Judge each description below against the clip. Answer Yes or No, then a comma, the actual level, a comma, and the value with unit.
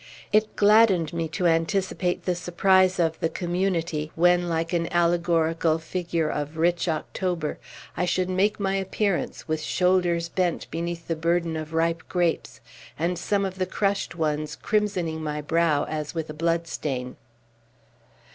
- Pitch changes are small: Yes, narrow, 2.2 semitones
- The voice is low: No, medium, 170 Hz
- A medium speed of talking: Yes, average, 145 wpm